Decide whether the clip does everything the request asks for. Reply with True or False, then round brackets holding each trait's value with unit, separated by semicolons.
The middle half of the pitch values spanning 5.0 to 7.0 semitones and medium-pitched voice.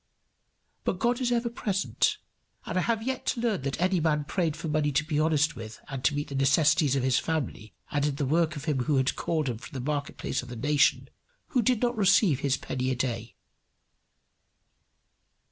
True (5.4 semitones; 150 Hz)